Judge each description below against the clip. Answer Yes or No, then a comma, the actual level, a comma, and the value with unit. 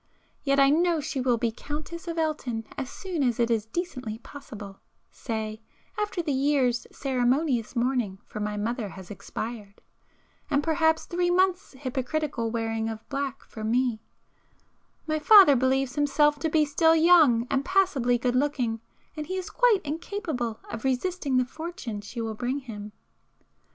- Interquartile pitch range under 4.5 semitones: No, wide, 5.4 semitones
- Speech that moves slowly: No, average, 150 wpm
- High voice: Yes, very high, 265 Hz